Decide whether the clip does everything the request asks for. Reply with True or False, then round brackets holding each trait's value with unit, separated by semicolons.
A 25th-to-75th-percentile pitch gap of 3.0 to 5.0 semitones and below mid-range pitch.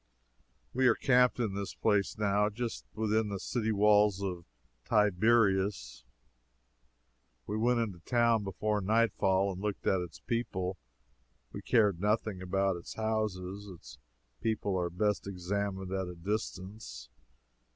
False (2.6 semitones; 100 Hz)